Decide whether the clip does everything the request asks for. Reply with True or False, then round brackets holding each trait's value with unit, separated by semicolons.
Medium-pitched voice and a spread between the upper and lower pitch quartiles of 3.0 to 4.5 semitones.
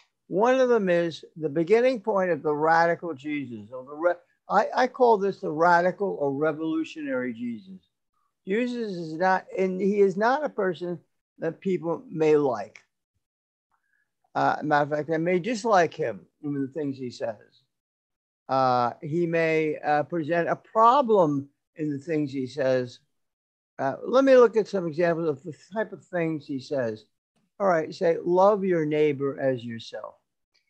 False (165 Hz; 5.1 semitones)